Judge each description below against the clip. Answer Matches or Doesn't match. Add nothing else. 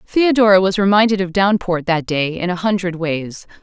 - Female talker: Matches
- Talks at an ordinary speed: Matches